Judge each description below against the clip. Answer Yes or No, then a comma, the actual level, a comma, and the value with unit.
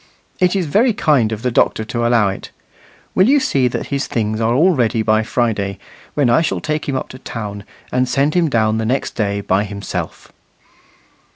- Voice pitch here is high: No, low, 120 Hz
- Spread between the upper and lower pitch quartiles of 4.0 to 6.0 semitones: Yes, average, 5.0 semitones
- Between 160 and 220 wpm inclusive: Yes, average, 200 wpm